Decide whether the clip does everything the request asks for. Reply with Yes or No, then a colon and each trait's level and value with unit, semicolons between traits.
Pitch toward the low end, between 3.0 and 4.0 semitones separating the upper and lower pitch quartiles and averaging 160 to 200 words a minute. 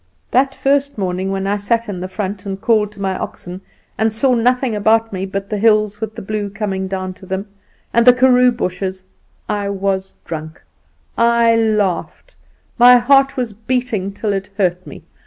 No: high, 210 Hz; average, 3.5 semitones; average, 180 wpm